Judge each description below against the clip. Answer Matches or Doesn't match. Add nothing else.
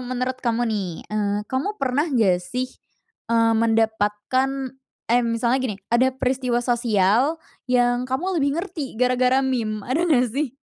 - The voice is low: Doesn't match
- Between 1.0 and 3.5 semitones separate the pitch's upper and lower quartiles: Matches